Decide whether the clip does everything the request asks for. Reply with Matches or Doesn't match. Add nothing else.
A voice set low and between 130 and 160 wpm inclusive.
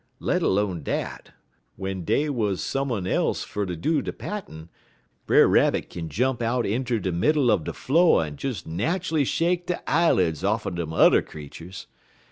Doesn't match